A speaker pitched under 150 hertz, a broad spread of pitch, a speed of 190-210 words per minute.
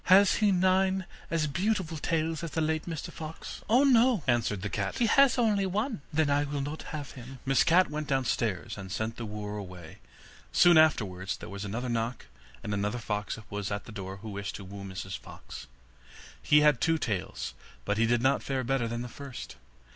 Yes: low, 135 Hz; wide, 7.8 semitones; average, 200 wpm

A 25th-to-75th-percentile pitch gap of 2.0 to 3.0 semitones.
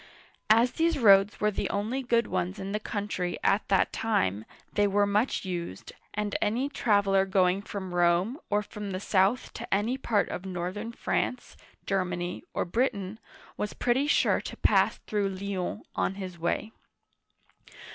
Yes: average, 2.7 semitones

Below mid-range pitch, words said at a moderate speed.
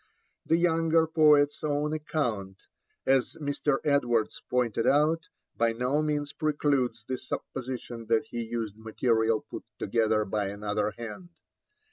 No: low, 125 Hz; slow, 125 wpm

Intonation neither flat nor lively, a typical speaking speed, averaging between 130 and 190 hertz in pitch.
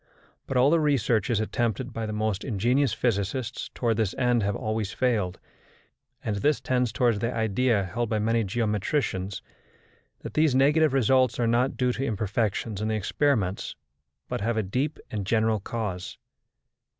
No: average, 3.3 semitones; average, 160 wpm; low, 115 Hz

